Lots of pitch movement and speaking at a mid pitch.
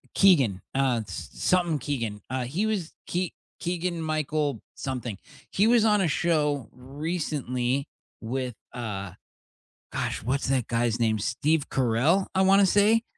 Yes: wide, 6.2 semitones; medium, 145 Hz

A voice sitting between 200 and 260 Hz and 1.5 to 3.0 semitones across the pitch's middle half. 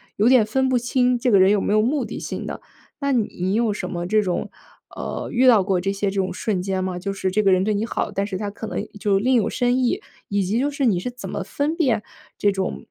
No: high, 210 Hz; average, 4.2 semitones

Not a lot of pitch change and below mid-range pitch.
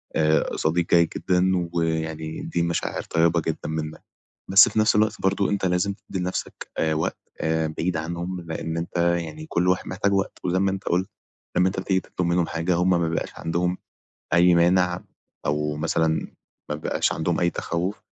Yes: narrow, 2.3 semitones; very low, 85 Hz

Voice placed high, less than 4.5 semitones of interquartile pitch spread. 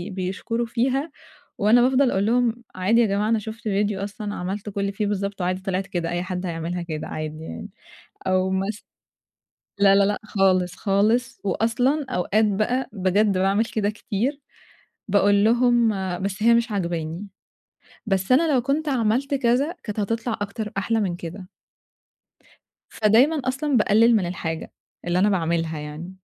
Yes: high, 205 Hz; average, 3.8 semitones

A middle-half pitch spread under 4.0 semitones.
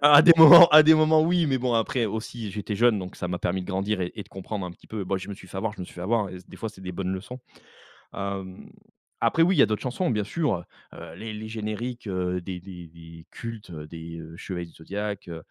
No: average, 4.7 semitones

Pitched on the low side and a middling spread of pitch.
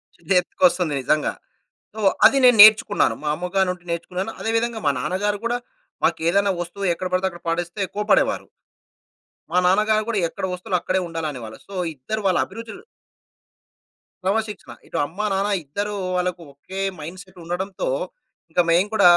No: high, 190 Hz; average, 3.2 semitones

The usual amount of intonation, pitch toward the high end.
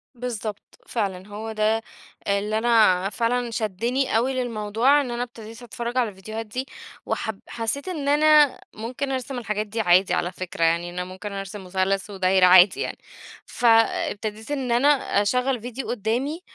Yes: average, 3.8 semitones; high, 225 Hz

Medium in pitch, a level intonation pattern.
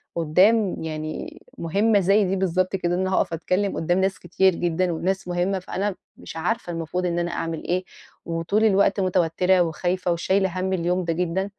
Yes: medium, 180 Hz; narrow, 2.1 semitones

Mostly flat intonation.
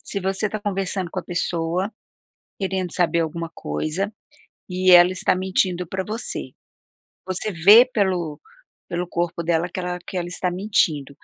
Yes: narrow, 2.1 semitones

